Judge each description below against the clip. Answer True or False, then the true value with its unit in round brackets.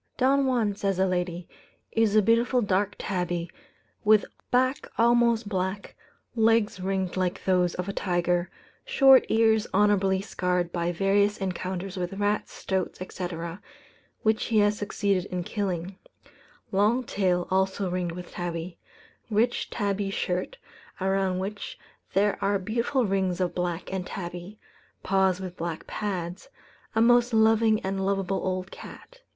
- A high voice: True (195 Hz)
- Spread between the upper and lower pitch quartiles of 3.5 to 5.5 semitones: False (2.9 semitones)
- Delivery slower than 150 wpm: True (140 wpm)